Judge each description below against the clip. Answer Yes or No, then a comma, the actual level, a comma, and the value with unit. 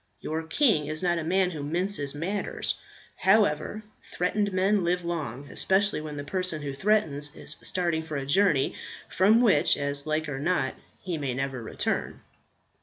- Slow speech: No, average, 165 wpm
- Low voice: No, medium, 160 Hz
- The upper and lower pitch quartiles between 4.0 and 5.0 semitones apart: Yes, average, 4.6 semitones